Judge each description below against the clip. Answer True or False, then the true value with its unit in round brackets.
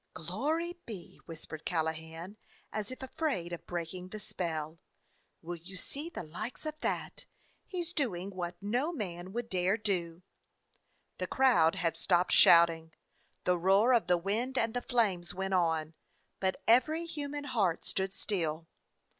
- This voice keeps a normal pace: True (150 wpm)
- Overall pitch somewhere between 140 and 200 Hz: True (190 Hz)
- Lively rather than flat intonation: True (6.2 semitones)